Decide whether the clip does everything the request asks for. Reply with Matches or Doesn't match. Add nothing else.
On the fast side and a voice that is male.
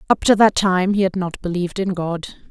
Doesn't match